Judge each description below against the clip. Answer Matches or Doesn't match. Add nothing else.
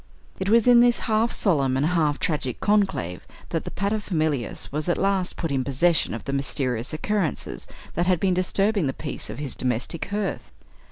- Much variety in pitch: Matches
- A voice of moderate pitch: Matches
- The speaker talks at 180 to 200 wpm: Matches